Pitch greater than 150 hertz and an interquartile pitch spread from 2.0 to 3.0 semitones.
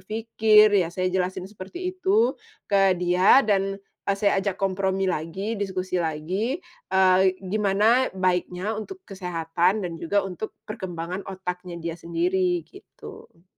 Yes: high, 190 Hz; narrow, 2.6 semitones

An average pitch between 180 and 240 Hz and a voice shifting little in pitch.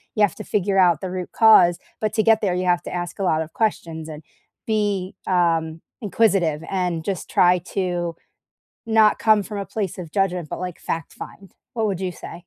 No: medium, 185 Hz; average, 3.1 semitones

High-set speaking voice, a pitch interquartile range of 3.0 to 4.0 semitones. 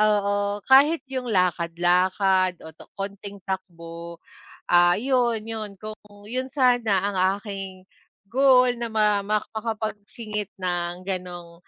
Yes: high, 200 Hz; average, 3.4 semitones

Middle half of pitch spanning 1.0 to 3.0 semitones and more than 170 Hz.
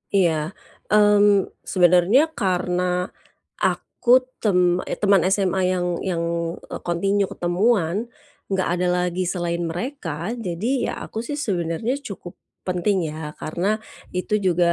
Yes: average, 2.7 semitones; medium, 185 Hz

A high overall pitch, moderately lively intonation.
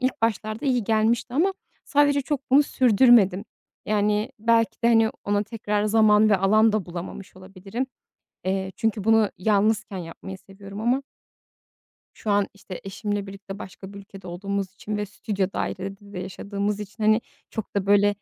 No: high, 205 Hz; narrow, 2.3 semitones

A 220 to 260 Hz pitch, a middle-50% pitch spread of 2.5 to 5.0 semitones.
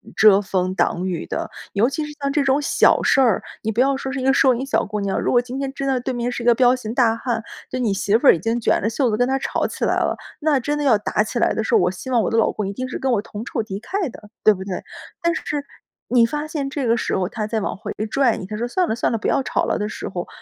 Yes: high, 240 Hz; average, 4.1 semitones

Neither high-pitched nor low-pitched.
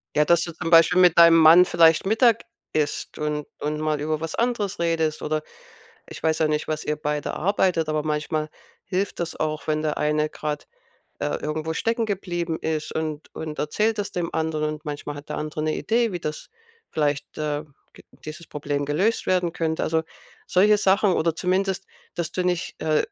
Yes: medium, 160 Hz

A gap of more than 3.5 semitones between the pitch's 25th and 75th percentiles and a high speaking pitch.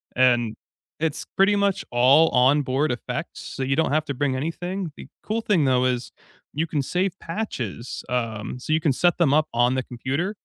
No: average, 4.8 semitones; medium, 140 Hz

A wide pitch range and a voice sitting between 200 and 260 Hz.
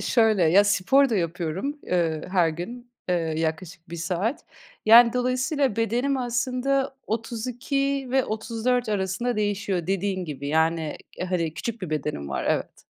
Yes: wide, 6.3 semitones; high, 210 Hz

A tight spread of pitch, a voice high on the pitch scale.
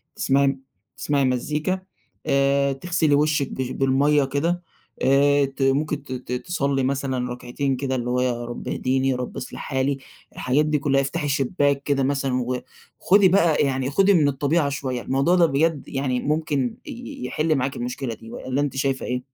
No: narrow, 2.1 semitones; medium, 140 Hz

